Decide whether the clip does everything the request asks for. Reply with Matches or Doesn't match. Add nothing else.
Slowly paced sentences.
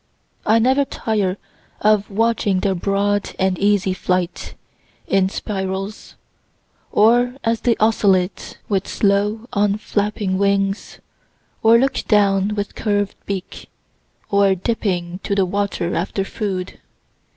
Matches